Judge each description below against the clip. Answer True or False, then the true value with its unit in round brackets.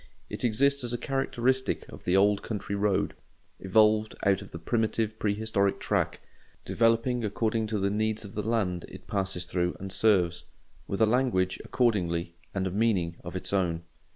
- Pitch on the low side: True (105 Hz)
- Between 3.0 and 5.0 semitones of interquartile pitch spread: True (3.3 semitones)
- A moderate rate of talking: True (170 wpm)